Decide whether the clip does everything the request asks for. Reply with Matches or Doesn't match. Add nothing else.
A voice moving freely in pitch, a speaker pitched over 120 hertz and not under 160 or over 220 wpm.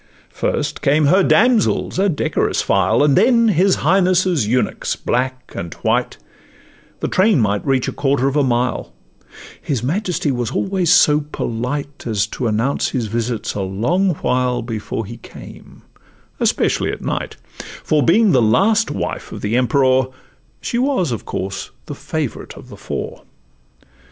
Doesn't match